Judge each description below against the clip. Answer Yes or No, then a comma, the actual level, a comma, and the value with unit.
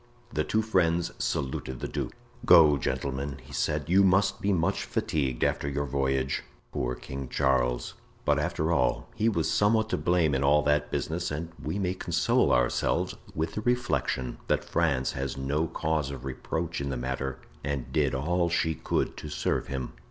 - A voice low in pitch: Yes, very low, 75 Hz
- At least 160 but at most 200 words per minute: Yes, average, 175 wpm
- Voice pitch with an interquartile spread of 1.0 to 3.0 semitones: No, average, 4.1 semitones